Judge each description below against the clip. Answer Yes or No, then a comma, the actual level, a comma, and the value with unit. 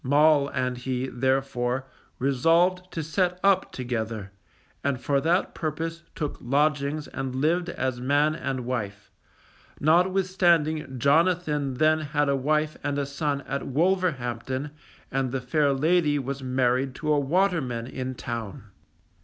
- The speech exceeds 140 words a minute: No, slow, 135 wpm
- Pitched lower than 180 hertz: Yes, medium, 140 Hz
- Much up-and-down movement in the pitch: No, average, 3.5 semitones